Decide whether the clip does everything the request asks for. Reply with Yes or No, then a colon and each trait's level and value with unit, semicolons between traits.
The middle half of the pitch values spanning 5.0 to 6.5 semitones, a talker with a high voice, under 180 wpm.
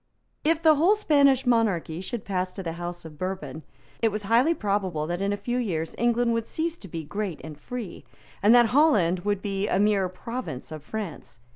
No: wide, 5.5 semitones; high, 205 Hz; average, 200 wpm